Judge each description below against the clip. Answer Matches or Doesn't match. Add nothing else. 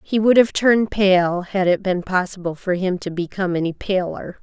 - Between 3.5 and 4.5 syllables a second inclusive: Doesn't match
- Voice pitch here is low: Doesn't match